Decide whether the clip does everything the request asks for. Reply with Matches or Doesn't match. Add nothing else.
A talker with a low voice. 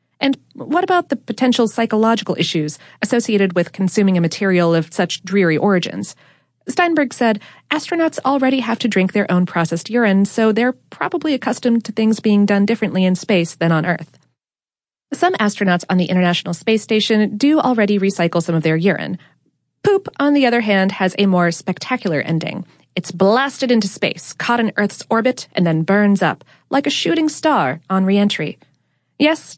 Doesn't match